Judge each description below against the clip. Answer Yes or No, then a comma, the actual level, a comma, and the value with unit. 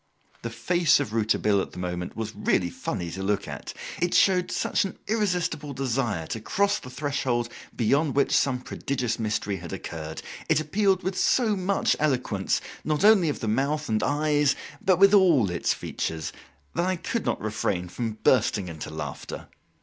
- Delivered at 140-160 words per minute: No, average, 170 wpm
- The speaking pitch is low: Yes, low, 130 Hz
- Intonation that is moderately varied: No, wide, 8.8 semitones